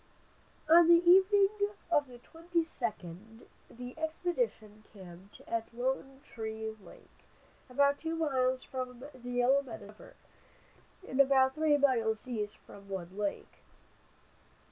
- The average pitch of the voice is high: Yes, very high, 255 Hz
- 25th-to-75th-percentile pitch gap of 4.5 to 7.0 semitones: Yes, average, 5.2 semitones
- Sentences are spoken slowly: Yes, slow, 120 wpm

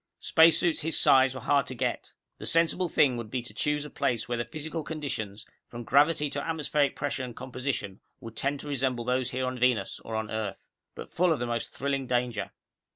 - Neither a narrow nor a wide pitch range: Yes, average, 3.7 semitones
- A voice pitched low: Yes, low, 130 Hz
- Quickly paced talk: Yes, fast, 210 wpm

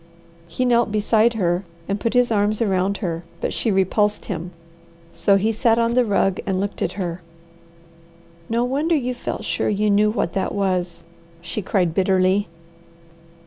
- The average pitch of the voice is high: Yes, high, 205 Hz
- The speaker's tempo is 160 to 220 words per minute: Yes, average, 165 wpm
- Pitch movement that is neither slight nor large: Yes, average, 3.5 semitones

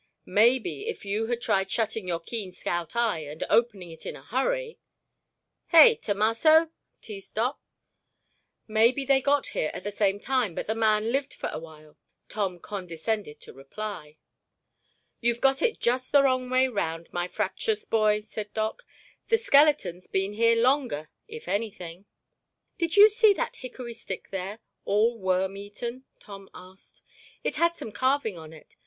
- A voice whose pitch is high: Yes, high, 220 Hz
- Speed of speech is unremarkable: Yes, average, 160 wpm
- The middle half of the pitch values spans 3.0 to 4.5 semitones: No, average, 5.2 semitones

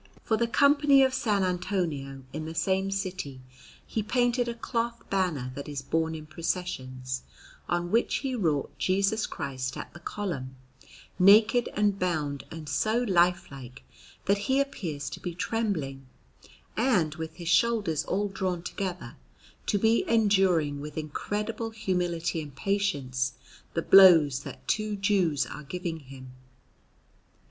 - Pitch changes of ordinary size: No, wide, 5.8 semitones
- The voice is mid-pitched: Yes, medium, 180 Hz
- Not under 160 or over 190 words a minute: No, average, 140 wpm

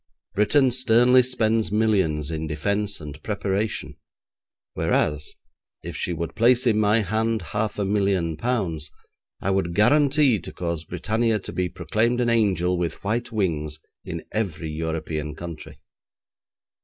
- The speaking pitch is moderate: No, low, 100 Hz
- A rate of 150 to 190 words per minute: No, slow, 135 wpm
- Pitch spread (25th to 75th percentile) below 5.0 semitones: No, average, 5.3 semitones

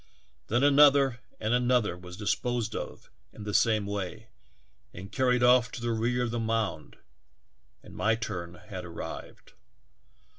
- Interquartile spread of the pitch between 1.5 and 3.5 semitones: Yes, average, 3.2 semitones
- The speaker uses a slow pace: No, average, 150 wpm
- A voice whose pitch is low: Yes, low, 115 Hz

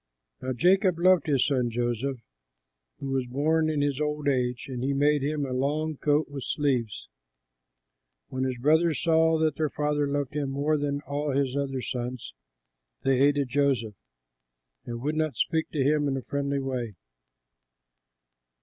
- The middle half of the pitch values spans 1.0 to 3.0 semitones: Yes, narrow, 2.5 semitones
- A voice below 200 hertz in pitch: Yes, medium, 140 Hz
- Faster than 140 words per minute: Yes, average, 160 wpm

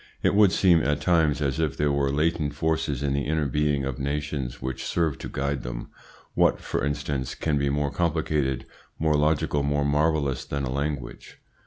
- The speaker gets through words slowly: No, average, 185 wpm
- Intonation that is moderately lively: No, narrow, 2.0 semitones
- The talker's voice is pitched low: Yes, very low, 70 Hz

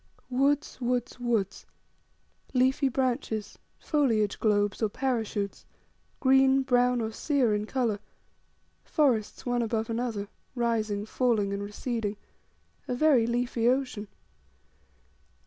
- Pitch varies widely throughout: No, average, 3.2 semitones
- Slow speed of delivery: Yes, slow, 105 wpm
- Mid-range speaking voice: No, high, 240 Hz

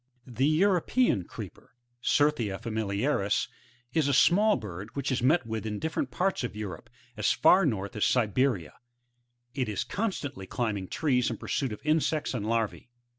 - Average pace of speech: Yes, average, 170 wpm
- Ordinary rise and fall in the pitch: No, wide, 6.2 semitones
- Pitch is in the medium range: No, low, 125 Hz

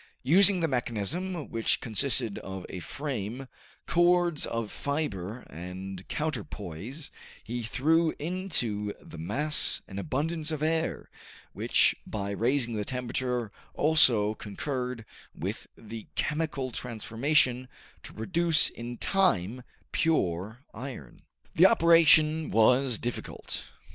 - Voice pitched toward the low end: Yes, low, 125 Hz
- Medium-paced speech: No, slow, 110 wpm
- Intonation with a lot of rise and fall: Yes, wide, 6.5 semitones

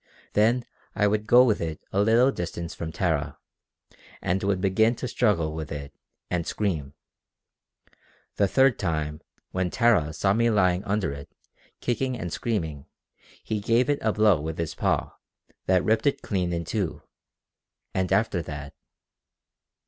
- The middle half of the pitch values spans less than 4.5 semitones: No, average, 5.3 semitones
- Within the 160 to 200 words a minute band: No, average, 150 wpm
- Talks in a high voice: No, very low, 95 Hz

